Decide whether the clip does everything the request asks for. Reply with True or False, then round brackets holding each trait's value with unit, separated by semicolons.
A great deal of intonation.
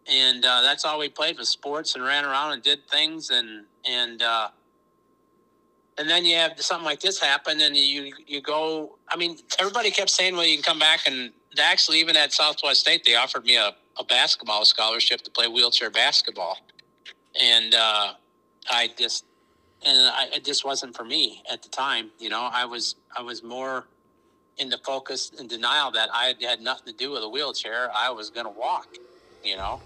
False (4.3 semitones)